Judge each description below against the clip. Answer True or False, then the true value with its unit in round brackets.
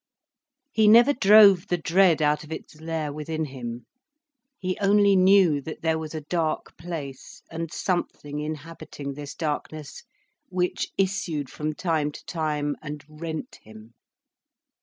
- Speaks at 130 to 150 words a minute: True (140 wpm)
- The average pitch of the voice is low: False (160 Hz)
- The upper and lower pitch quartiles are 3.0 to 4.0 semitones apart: True (3.4 semitones)